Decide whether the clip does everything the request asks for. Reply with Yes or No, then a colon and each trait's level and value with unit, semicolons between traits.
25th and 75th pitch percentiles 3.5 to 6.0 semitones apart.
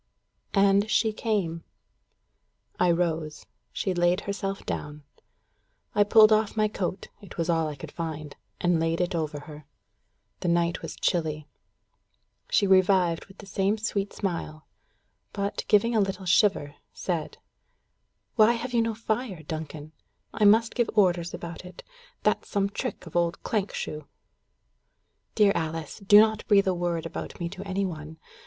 Yes: average, 3.9 semitones